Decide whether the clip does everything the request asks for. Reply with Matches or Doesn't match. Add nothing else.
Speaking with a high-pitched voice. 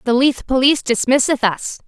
Matches